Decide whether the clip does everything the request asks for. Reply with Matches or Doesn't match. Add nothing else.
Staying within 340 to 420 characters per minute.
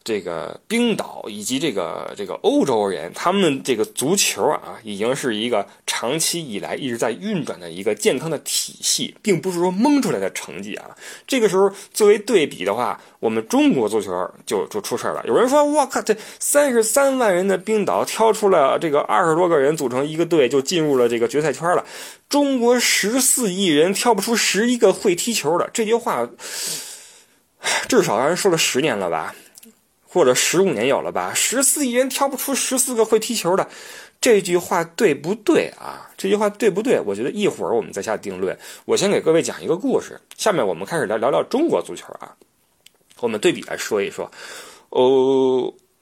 Doesn't match